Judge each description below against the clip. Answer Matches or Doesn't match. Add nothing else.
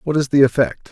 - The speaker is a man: Matches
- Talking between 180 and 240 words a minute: Doesn't match